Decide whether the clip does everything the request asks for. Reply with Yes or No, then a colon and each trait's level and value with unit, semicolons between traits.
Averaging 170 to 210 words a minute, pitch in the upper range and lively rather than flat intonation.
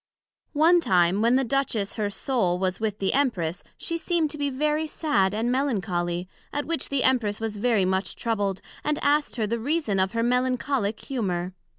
Yes: average, 185 wpm; high, 230 Hz; wide, 6.3 semitones